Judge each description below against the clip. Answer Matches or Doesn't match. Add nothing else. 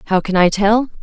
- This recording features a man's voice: Doesn't match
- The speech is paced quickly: Matches